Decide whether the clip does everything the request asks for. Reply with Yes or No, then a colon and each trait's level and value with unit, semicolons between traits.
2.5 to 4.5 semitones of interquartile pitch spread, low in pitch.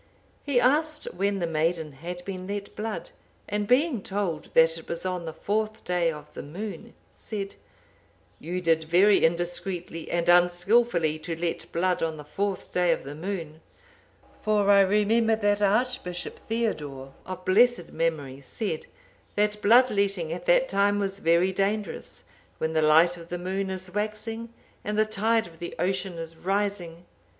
No: average, 3.9 semitones; medium, 185 Hz